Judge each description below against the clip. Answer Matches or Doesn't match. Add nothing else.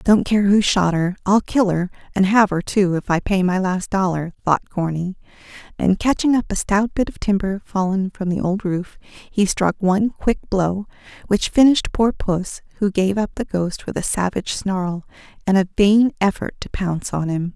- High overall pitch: Matches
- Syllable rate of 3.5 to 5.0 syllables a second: Matches